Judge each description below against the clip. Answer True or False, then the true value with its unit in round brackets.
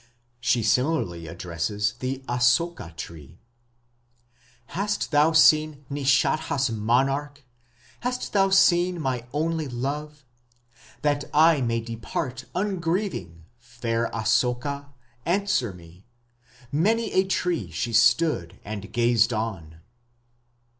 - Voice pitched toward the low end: True (130 Hz)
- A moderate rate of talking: False (100 wpm)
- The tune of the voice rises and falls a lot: True (5.9 semitones)